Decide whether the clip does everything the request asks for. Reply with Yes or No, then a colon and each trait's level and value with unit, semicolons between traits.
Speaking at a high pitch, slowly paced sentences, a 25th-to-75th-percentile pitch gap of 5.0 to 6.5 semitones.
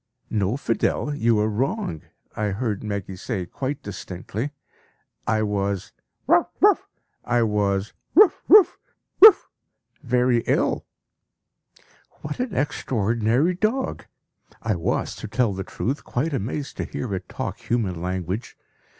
No: low, 115 Hz; slow, 125 wpm; average, 5.3 semitones